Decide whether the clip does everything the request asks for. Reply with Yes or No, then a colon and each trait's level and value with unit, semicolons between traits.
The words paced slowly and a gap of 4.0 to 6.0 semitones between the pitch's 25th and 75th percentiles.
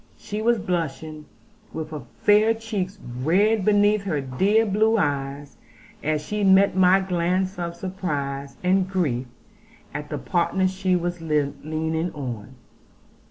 Yes: slow, 130 wpm; average, 4.5 semitones